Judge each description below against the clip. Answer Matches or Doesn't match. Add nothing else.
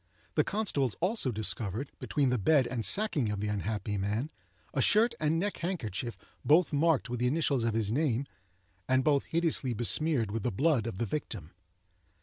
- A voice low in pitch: Matches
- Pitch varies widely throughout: Matches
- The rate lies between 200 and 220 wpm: Doesn't match